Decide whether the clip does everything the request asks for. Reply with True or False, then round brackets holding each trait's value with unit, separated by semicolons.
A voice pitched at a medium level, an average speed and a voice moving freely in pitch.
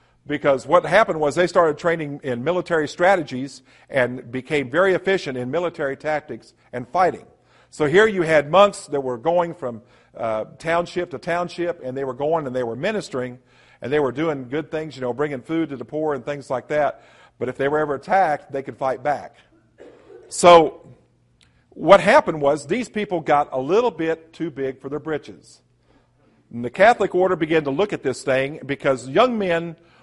False (150 Hz; 190 wpm; 4.6 semitones)